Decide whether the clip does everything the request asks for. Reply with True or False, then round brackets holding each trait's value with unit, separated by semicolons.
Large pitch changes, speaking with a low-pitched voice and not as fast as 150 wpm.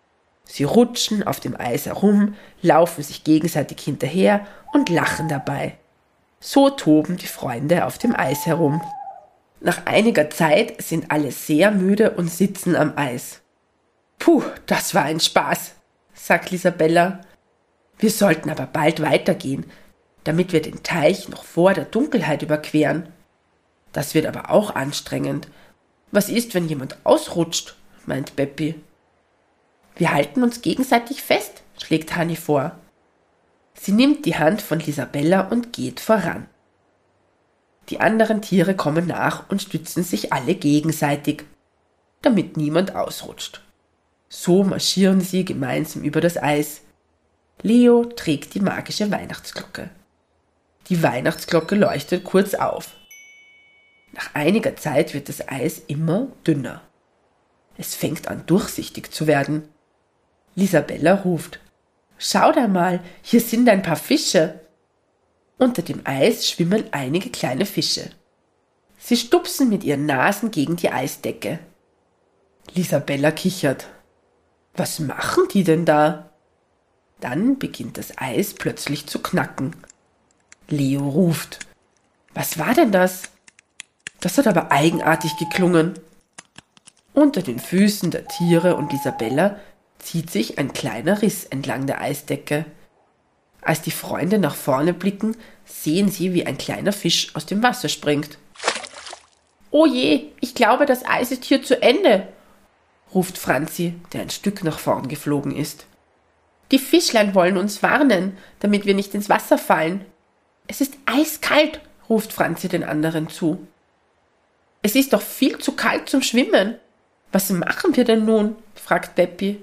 False (5.9 semitones; 175 Hz; 130 wpm)